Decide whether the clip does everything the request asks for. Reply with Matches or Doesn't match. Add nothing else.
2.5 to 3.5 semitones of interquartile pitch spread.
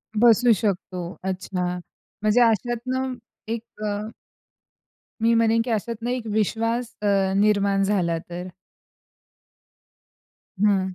Matches